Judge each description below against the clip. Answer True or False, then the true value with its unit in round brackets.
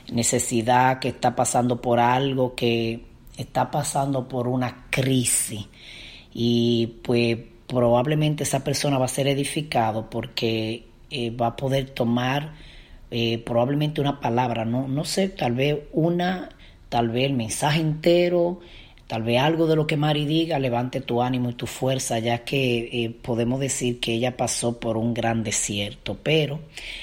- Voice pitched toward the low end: True (125 Hz)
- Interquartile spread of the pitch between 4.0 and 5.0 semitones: False (3.2 semitones)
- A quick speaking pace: False (155 wpm)